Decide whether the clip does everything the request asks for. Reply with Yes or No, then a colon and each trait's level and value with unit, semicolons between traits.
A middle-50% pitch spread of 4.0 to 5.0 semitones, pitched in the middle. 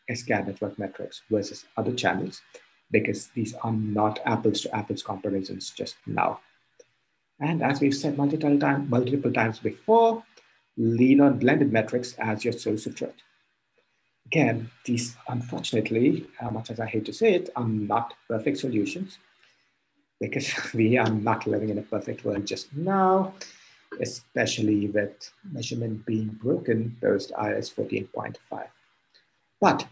No: average, 4.5 semitones; low, 115 Hz